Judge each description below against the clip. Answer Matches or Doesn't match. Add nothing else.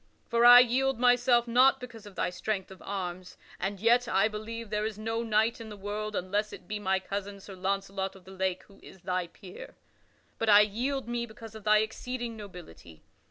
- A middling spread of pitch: Matches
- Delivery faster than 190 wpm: Matches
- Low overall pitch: Doesn't match